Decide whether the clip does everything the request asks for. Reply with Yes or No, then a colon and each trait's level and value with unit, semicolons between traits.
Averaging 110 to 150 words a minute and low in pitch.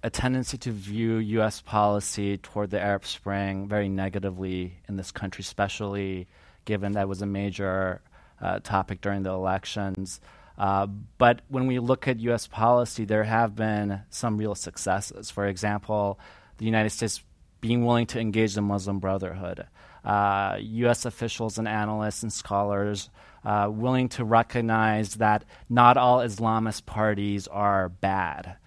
Yes: average, 145 wpm; low, 105 Hz